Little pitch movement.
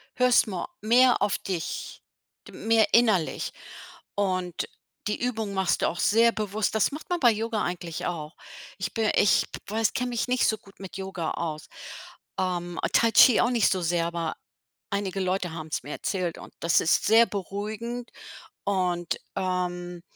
No: average, 4.1 semitones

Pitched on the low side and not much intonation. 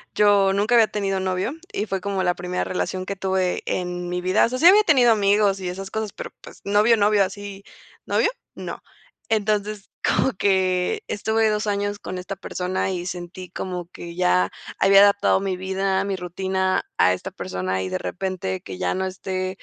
No: high, 190 Hz; narrow, 2.1 semitones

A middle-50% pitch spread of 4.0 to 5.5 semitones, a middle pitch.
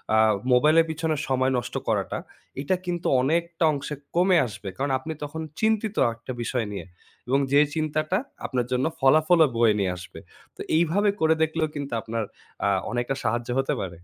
Yes: average, 4.8 semitones; medium, 145 Hz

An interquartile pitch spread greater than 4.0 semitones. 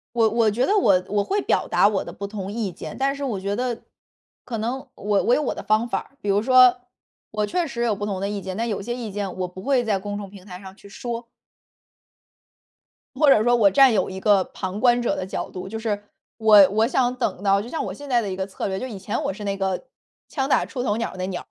No: average, 3.6 semitones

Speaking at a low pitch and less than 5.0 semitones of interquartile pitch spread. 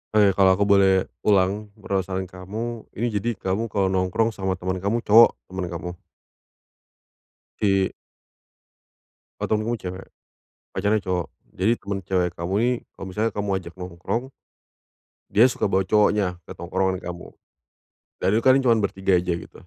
Yes: very low, 95 Hz; narrow, 2.4 semitones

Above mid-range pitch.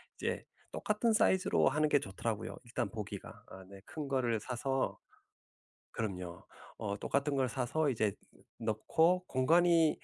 No: low, 130 Hz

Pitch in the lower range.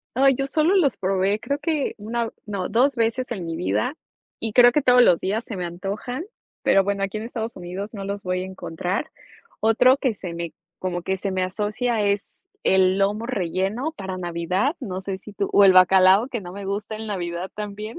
No: high, 200 Hz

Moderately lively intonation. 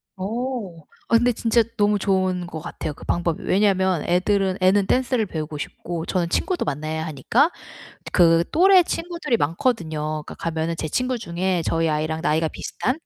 No: wide, 6.0 semitones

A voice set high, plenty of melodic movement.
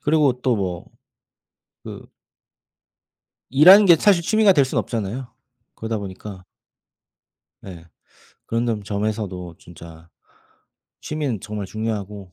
No: low, 110 Hz; wide, 6.3 semitones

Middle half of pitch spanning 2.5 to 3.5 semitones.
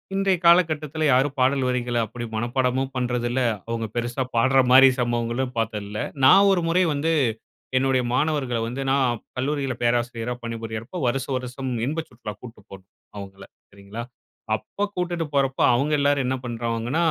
Yes: average, 3.1 semitones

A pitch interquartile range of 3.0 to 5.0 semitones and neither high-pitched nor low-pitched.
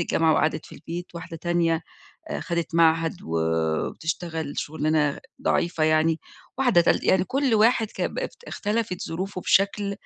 Yes: average, 3.6 semitones; medium, 170 Hz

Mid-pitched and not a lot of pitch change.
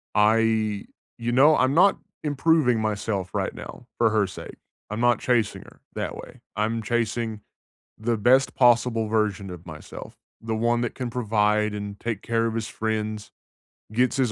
No: low, 110 Hz; narrow, 2.2 semitones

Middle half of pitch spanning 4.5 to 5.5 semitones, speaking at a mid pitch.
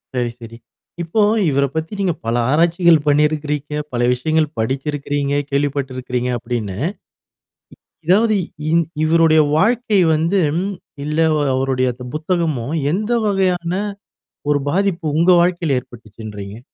Yes: average, 4.9 semitones; medium, 150 Hz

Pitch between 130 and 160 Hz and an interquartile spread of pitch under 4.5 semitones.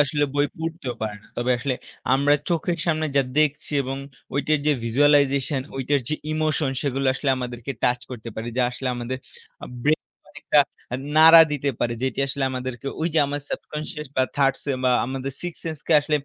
Yes: medium, 140 Hz; average, 2.9 semitones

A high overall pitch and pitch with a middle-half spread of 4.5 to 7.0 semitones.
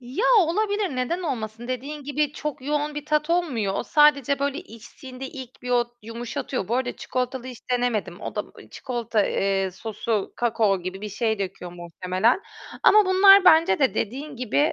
Yes: very high, 250 Hz; average, 5.3 semitones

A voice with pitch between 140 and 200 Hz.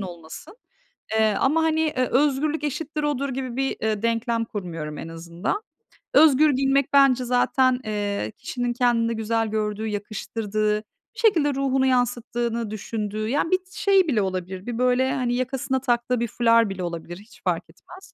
No: high, 240 Hz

